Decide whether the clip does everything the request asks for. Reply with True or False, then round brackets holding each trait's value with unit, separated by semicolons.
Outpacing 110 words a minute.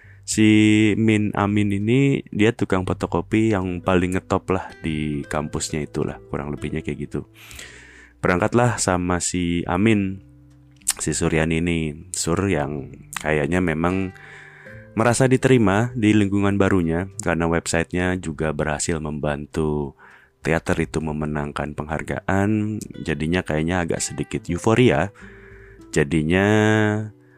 False (105 wpm)